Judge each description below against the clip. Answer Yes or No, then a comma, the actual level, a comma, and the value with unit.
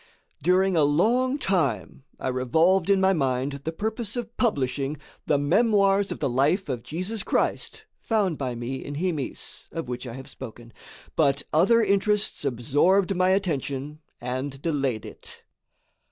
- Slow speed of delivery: No, average, 150 wpm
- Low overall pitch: No, medium, 155 Hz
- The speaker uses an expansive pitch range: Yes, wide, 6.6 semitones